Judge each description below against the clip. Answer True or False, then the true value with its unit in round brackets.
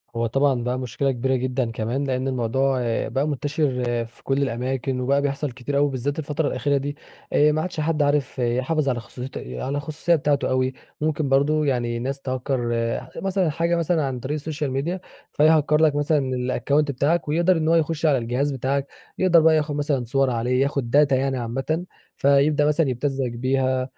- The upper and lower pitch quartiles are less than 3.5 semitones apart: True (2.8 semitones)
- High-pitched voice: False (140 Hz)